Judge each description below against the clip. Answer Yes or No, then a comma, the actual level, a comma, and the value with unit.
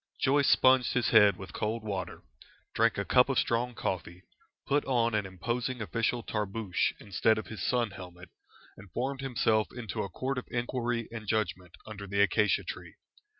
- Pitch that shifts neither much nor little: Yes, average, 3.5 semitones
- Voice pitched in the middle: No, low, 110 Hz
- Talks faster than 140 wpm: Yes, average, 170 wpm